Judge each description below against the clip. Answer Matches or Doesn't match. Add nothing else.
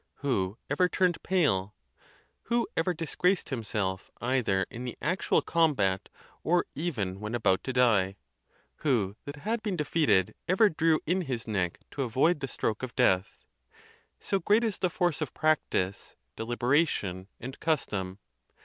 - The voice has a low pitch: Matches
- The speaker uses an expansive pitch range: Matches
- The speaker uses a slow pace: Doesn't match